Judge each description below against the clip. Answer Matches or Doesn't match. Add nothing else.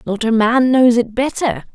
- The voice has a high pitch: Matches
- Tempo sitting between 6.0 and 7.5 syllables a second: Doesn't match